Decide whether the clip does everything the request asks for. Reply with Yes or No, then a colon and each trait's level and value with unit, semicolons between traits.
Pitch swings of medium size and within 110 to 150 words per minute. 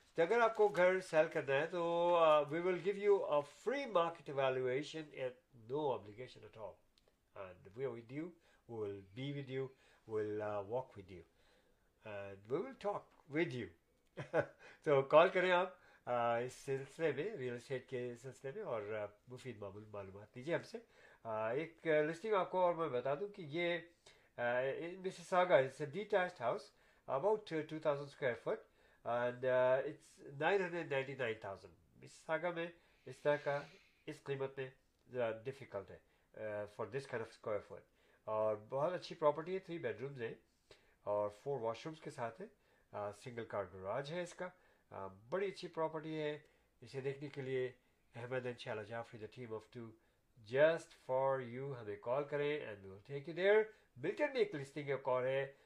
No: wide, 6.0 semitones; average, 120 wpm